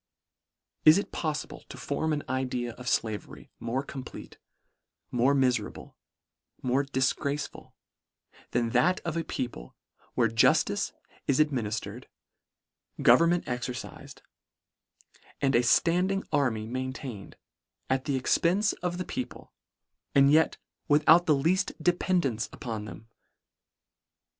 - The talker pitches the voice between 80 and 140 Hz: Yes, low, 135 Hz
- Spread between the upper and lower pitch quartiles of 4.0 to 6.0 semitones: Yes, average, 4.6 semitones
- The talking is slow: Yes, slow, 120 wpm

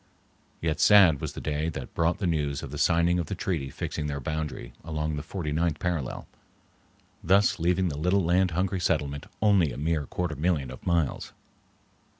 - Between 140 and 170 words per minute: No, average, 180 wpm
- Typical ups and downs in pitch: Yes, average, 3.3 semitones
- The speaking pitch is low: Yes, very low, 80 Hz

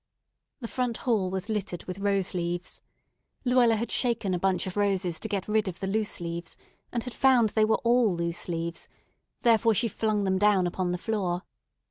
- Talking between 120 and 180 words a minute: No, average, 190 wpm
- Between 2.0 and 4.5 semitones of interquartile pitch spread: Yes, average, 3.8 semitones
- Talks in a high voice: Yes, high, 200 Hz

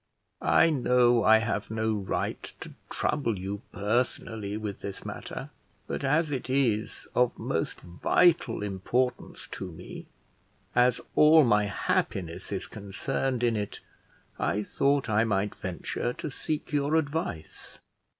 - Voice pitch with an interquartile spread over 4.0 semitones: Yes, average, 4.9 semitones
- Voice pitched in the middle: No, low, 115 Hz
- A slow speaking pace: Yes, slow, 130 wpm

